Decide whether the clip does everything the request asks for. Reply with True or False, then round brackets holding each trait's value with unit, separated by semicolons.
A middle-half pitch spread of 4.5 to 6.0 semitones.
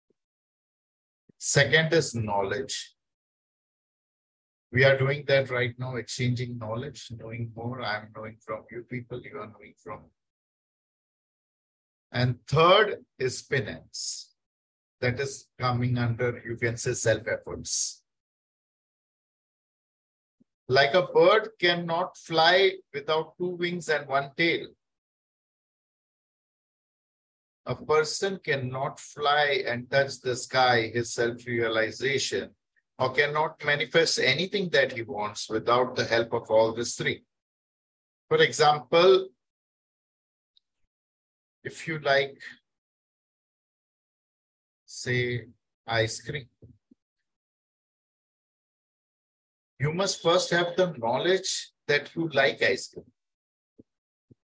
True (5.2 semitones)